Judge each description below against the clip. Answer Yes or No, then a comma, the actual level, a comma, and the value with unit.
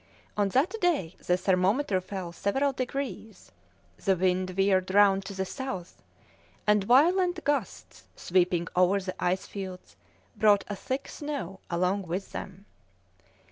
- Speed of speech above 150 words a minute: No, slow, 135 wpm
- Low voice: No, high, 195 Hz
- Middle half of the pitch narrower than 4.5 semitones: No, wide, 5.6 semitones